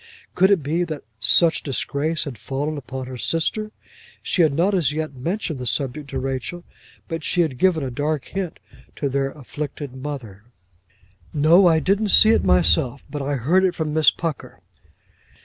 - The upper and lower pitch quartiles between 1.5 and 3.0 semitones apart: No, average, 4.1 semitones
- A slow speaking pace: No, average, 175 wpm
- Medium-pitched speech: Yes, medium, 150 Hz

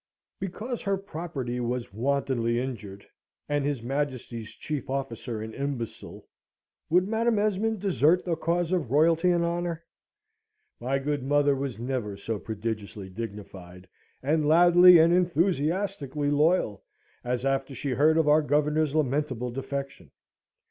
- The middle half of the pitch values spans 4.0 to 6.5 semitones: Yes, wide, 5.6 semitones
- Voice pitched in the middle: Yes, medium, 145 Hz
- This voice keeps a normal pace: No, slow, 130 wpm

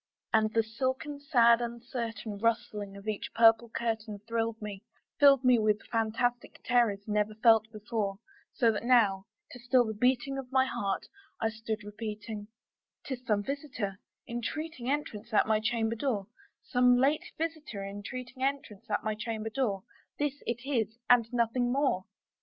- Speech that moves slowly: No, average, 155 wpm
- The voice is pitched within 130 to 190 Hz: No, high, 230 Hz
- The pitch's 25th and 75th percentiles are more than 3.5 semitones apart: No, average, 2.8 semitones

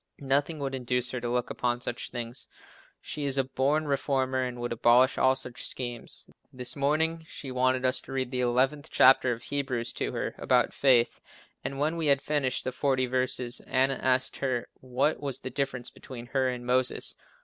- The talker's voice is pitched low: Yes, low, 130 Hz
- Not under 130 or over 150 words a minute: No, average, 190 wpm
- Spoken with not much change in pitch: Yes, narrow, 1.7 semitones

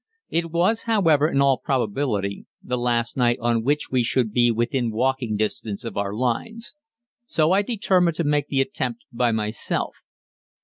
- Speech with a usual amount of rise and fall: No, wide, 5.8 semitones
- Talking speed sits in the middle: Yes, average, 165 wpm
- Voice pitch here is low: Yes, low, 130 Hz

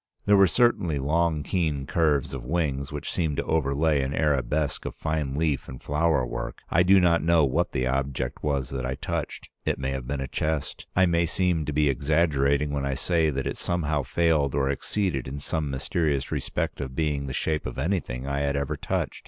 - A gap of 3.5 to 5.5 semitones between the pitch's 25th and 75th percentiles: No, average, 3.1 semitones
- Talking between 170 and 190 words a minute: No, fast, 205 wpm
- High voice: No, very low, 75 Hz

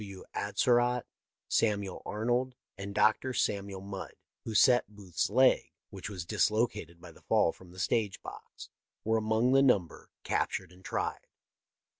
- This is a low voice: Yes, low, 105 Hz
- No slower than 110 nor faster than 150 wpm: Yes, average, 145 wpm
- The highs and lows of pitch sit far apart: No, average, 3.9 semitones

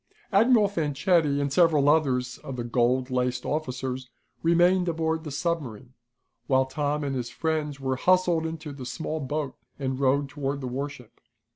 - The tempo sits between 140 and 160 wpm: Yes, average, 155 wpm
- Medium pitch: Yes, medium, 145 Hz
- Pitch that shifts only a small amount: No, average, 3.6 semitones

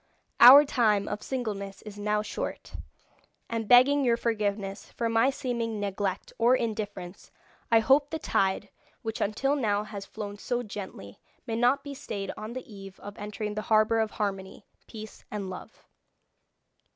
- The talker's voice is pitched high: Yes, high, 215 Hz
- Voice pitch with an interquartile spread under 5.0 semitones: Yes, average, 2.9 semitones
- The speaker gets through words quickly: No, average, 155 wpm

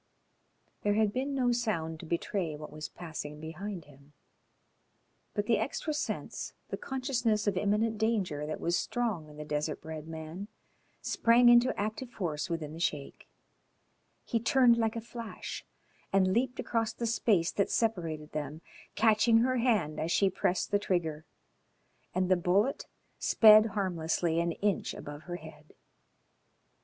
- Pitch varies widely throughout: Yes, wide, 6.1 semitones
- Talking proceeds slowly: No, average, 150 wpm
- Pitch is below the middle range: No, high, 190 Hz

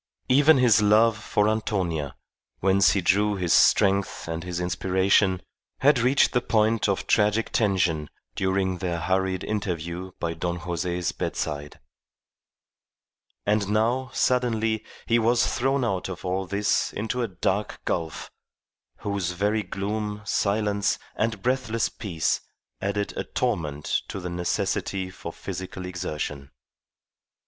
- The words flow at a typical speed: No, slow, 125 wpm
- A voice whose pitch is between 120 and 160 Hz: No, low, 100 Hz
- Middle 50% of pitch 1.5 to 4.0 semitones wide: Yes, average, 3.4 semitones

